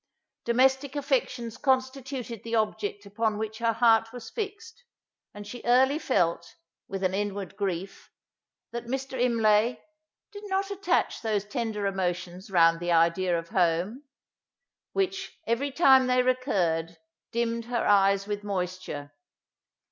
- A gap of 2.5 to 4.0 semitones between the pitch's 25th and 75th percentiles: No, average, 5.0 semitones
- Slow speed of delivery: Yes, slow, 130 wpm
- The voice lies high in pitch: Yes, high, 225 Hz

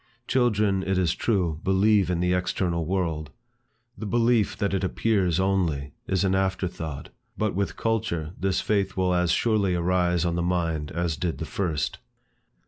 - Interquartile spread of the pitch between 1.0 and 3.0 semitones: Yes, narrow, 2.5 semitones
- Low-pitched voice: Yes, very low, 90 Hz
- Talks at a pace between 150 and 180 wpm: Yes, average, 160 wpm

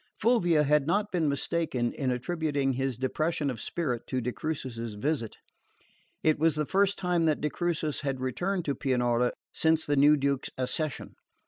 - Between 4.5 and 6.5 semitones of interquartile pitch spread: No, average, 4.0 semitones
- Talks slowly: No, average, 165 wpm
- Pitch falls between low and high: Yes, medium, 150 Hz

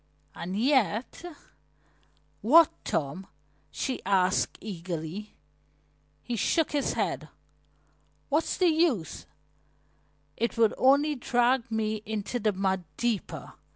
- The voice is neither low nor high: No, high, 220 Hz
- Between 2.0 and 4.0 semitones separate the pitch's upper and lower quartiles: No, wide, 5.5 semitones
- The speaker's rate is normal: No, slow, 105 wpm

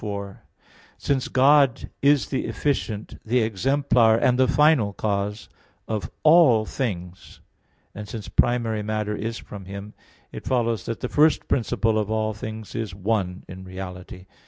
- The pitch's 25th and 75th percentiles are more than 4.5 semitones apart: No, average, 3.7 semitones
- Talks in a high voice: No, low, 110 Hz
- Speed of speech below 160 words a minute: Yes, average, 145 wpm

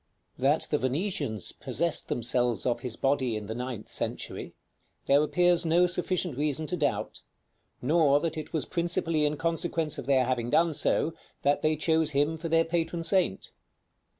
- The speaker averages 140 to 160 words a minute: No, average, 175 wpm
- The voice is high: No, medium, 150 Hz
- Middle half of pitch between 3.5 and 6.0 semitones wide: Yes, average, 4.2 semitones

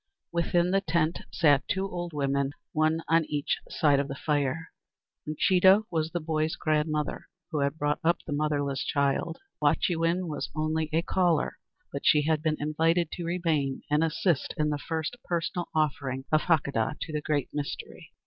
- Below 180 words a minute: Yes, average, 170 wpm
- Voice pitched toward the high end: No, medium, 155 Hz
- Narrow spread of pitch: Yes, narrow, 2.3 semitones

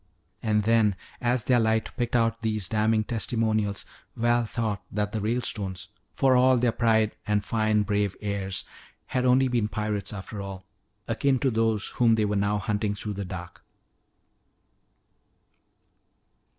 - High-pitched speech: No, low, 110 Hz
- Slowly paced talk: No, average, 145 wpm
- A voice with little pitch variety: Yes, narrow, 2.1 semitones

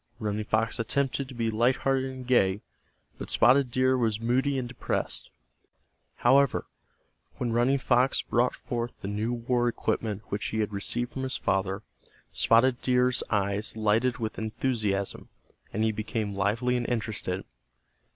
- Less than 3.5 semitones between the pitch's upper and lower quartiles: Yes, average, 2.9 semitones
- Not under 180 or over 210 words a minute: No, average, 150 wpm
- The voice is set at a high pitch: No, low, 115 Hz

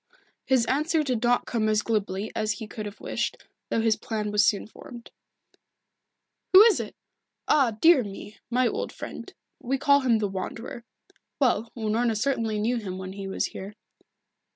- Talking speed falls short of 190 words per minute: Yes, average, 170 wpm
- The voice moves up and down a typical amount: Yes, average, 3.1 semitones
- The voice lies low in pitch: No, high, 225 Hz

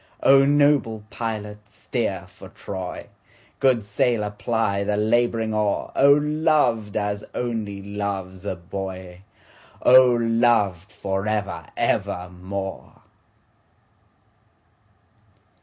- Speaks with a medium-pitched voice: No, low, 105 Hz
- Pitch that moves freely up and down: No, average, 3.3 semitones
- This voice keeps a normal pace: No, slow, 80 wpm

